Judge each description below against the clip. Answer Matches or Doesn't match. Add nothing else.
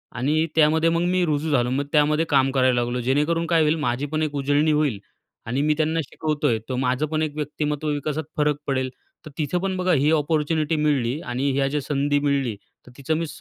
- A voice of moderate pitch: Matches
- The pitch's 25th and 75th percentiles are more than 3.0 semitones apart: Doesn't match